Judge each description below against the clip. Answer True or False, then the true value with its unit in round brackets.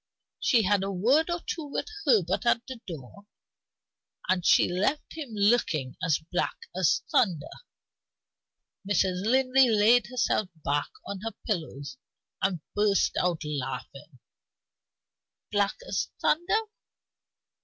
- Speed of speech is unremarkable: False (120 wpm)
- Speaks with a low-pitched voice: False (200 Hz)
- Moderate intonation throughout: False (6.3 semitones)